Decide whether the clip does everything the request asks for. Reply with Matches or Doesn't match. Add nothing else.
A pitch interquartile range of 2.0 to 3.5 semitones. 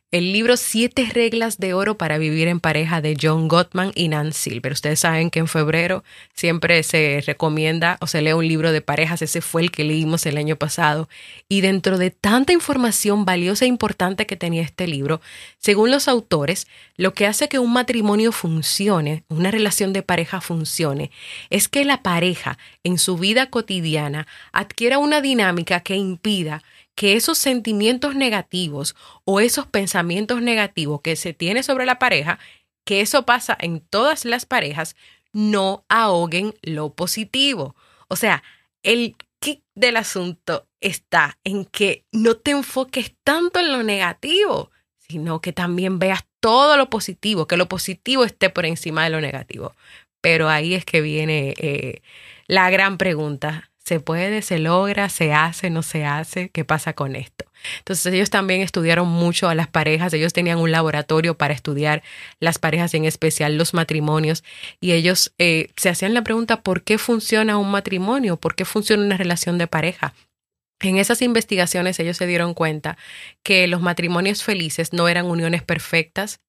Doesn't match